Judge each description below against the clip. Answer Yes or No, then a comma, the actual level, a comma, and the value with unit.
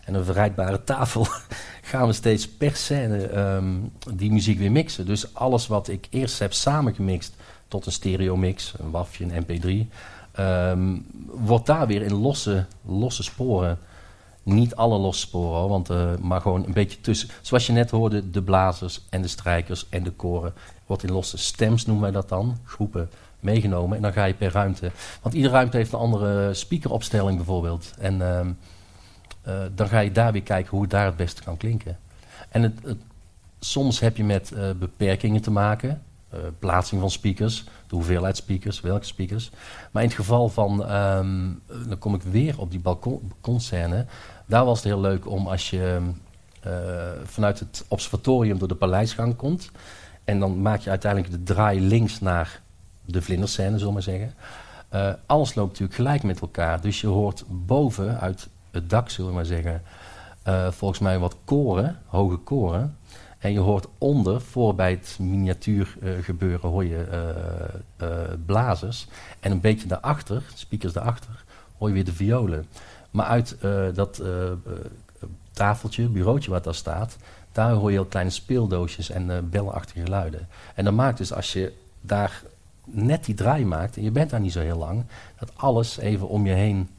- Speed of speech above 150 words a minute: Yes, average, 180 wpm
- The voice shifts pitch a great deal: No, average, 3.2 semitones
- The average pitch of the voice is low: Yes, low, 100 Hz